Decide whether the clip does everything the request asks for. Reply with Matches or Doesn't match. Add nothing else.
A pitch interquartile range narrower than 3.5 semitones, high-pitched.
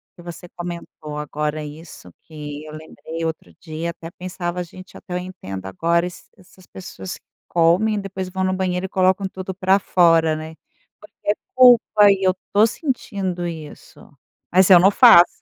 Doesn't match